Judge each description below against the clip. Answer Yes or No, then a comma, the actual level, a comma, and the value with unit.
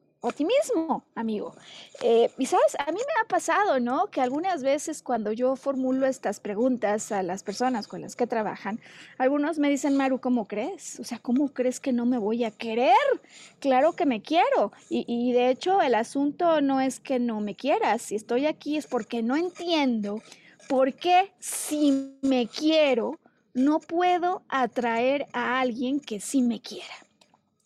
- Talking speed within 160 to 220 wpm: Yes, average, 170 wpm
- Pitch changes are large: No, average, 4.3 semitones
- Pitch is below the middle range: No, very high, 260 Hz